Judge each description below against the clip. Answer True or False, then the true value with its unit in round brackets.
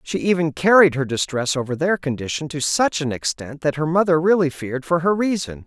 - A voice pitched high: False (155 Hz)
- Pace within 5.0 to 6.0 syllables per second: True (5.6 syllables/s)